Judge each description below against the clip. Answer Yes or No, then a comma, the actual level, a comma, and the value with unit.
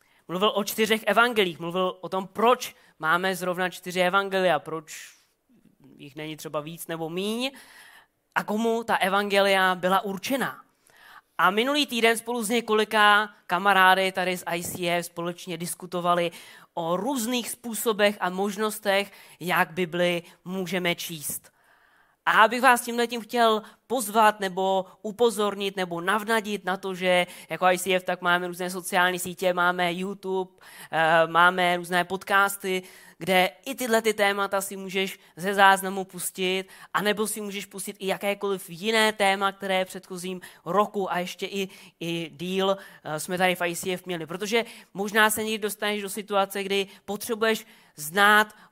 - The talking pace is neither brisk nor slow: Yes, average, 140 wpm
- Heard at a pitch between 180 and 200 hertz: Yes, high, 190 Hz